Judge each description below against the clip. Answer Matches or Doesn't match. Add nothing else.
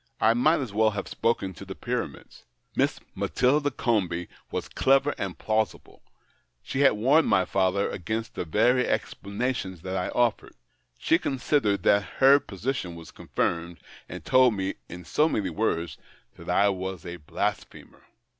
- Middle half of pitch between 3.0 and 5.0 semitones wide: Doesn't match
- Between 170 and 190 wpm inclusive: Doesn't match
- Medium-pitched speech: Doesn't match